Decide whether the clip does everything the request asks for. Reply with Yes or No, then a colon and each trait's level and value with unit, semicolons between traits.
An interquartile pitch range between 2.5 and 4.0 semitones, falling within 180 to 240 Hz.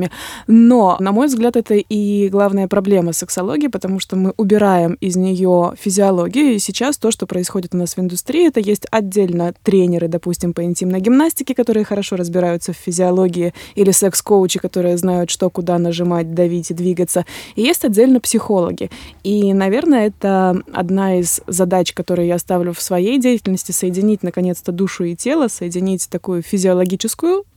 Yes: average, 2.9 semitones; high, 190 Hz